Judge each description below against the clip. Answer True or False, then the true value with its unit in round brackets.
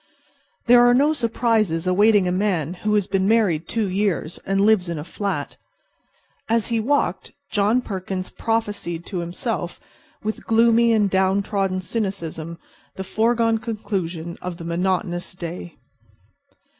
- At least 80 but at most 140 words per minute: True (135 wpm)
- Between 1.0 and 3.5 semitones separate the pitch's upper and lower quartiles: False (3.9 semitones)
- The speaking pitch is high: True (195 Hz)